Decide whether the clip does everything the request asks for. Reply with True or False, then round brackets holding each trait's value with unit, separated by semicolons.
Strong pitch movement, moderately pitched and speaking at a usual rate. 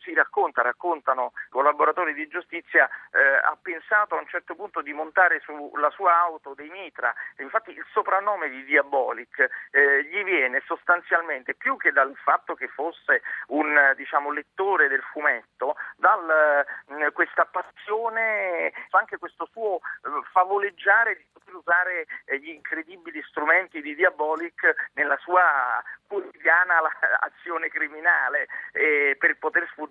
True (6.1 semitones; 175 Hz; 130 wpm)